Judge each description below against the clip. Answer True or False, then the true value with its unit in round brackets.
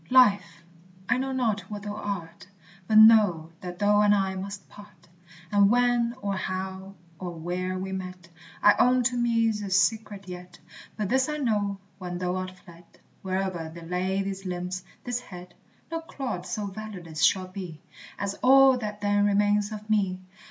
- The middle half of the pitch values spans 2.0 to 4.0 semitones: True (2.8 semitones)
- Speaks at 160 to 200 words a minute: True (170 wpm)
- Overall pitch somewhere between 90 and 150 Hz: False (200 Hz)